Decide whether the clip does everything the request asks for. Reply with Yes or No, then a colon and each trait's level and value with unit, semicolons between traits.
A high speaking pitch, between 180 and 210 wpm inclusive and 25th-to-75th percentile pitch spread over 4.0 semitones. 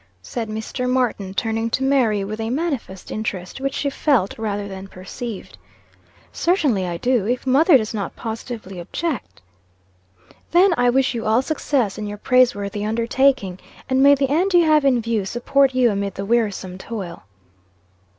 No: high, 230 Hz; average, 160 wpm; average, 4.8 semitones